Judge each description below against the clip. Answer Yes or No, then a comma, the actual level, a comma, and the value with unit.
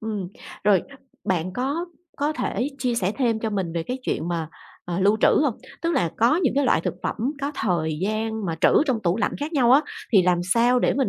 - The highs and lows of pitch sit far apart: Yes, wide, 6.1 semitones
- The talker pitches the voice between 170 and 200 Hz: No, high, 220 Hz